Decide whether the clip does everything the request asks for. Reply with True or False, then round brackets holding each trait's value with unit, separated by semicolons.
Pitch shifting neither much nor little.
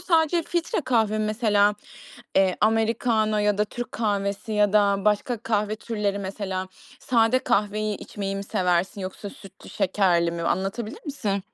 False (2.2 semitones)